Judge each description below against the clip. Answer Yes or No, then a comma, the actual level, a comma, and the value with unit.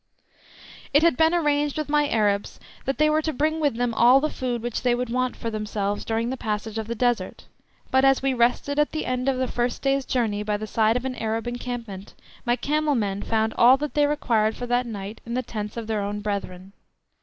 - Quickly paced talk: Yes, fast, 230 wpm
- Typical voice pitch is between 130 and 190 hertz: No, high, 240 Hz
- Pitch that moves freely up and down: No, average, 3.8 semitones